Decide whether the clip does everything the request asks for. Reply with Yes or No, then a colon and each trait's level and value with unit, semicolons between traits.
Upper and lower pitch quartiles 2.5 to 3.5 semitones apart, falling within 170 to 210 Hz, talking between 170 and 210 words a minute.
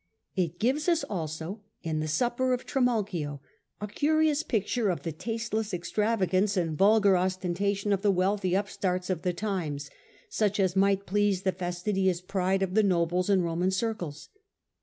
No: average, 3.1 semitones; high, 190 Hz; average, 160 wpm